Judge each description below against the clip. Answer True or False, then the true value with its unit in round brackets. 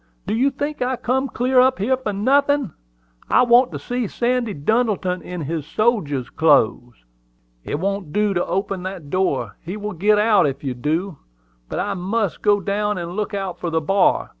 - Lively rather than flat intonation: True (5.7 semitones)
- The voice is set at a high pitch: True (200 Hz)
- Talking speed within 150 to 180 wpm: False (190 wpm)